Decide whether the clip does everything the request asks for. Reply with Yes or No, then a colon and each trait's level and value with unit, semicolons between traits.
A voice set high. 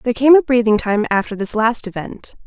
Yes: high, 230 Hz